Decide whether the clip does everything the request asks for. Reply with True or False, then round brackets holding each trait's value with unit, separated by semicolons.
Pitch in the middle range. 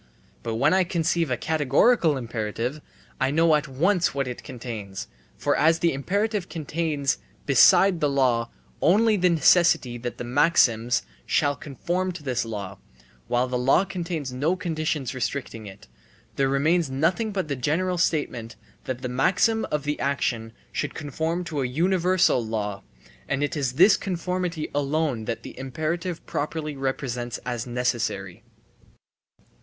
True (145 Hz)